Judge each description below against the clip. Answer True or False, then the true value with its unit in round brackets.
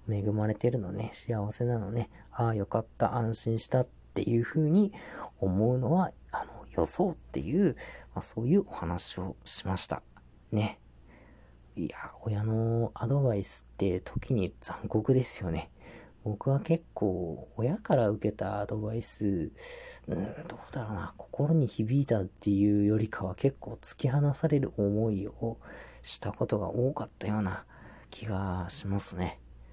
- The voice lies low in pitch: True (110 Hz)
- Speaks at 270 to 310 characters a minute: True (280 characters per minute)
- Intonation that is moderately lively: True (3.9 semitones)